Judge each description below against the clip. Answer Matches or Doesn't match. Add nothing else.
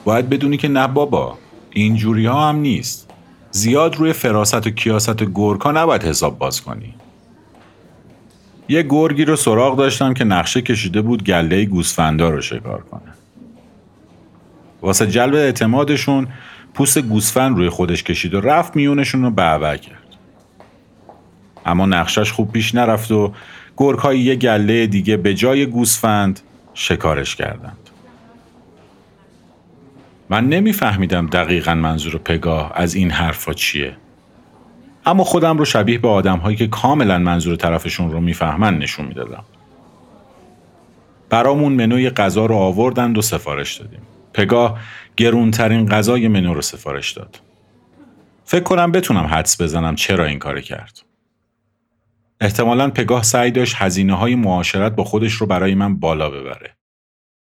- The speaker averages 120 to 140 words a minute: Matches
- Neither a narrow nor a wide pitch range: Matches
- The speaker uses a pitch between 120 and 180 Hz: Doesn't match